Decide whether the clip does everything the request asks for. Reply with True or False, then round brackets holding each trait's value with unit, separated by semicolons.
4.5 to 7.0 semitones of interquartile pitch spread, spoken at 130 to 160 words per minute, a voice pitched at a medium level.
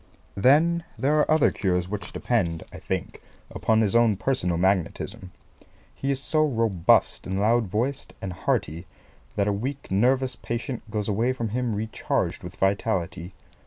False (5.1 semitones; 155 wpm; 110 Hz)